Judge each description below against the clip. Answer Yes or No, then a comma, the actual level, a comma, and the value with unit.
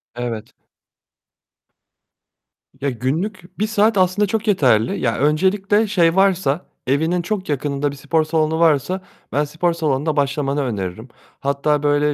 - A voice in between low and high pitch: Yes, medium, 155 Hz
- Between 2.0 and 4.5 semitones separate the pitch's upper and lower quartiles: No, average, 4.9 semitones